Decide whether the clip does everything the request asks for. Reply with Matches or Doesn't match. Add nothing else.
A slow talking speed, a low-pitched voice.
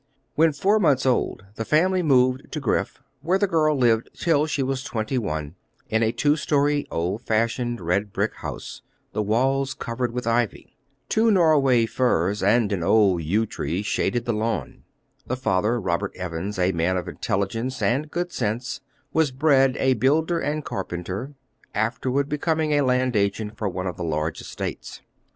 Doesn't match